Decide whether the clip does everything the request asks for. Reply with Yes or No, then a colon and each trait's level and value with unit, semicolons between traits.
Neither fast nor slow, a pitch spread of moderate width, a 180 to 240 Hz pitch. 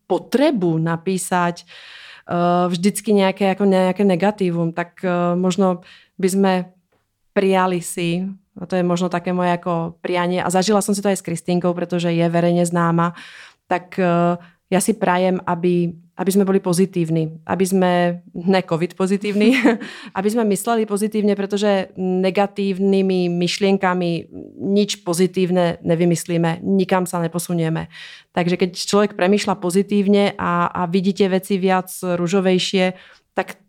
No: average, 135 wpm; narrow, 2.0 semitones; medium, 185 Hz